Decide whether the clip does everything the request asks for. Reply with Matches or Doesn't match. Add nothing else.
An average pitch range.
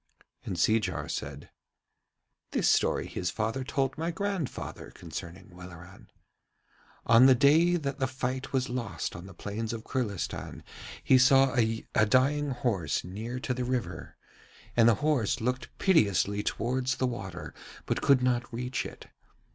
Matches